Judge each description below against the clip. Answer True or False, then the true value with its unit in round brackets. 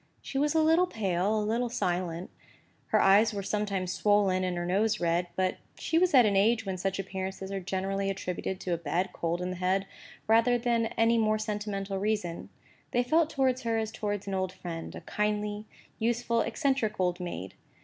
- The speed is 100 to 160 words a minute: False (195 wpm)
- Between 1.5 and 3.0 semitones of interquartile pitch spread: False (3.5 semitones)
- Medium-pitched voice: False (205 Hz)